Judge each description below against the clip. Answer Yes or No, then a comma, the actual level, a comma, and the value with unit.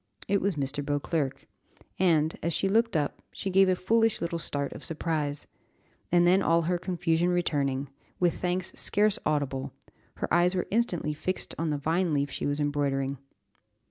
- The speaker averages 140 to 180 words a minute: Yes, average, 170 wpm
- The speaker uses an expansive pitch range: No, average, 4.1 semitones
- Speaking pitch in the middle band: Yes, medium, 165 Hz